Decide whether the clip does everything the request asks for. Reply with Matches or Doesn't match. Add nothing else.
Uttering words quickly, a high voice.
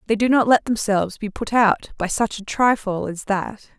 Matches